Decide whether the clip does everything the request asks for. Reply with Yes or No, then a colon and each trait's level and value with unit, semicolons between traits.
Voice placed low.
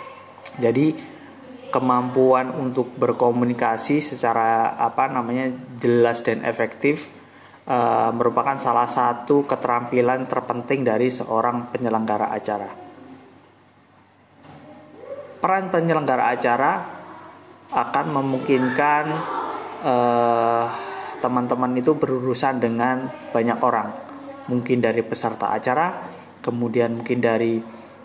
Yes: low, 125 Hz